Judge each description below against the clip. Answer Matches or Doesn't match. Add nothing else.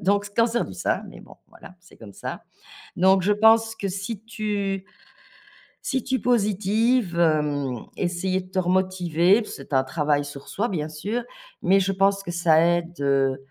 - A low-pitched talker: Doesn't match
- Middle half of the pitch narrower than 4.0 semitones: Doesn't match